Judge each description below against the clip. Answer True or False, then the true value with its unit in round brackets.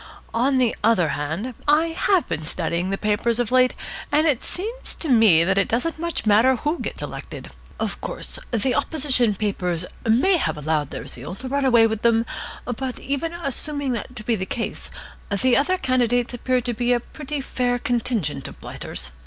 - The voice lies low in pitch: False (245 Hz)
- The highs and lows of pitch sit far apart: False (4.7 semitones)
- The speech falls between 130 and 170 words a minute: False (185 wpm)